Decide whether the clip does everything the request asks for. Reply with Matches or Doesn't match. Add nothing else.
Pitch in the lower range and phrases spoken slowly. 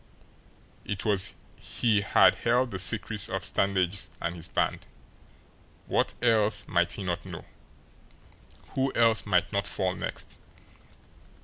Matches